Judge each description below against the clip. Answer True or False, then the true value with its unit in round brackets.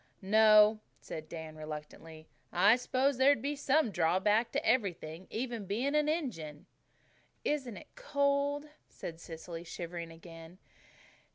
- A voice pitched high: True (210 Hz)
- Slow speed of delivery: True (120 wpm)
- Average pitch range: False (8.6 semitones)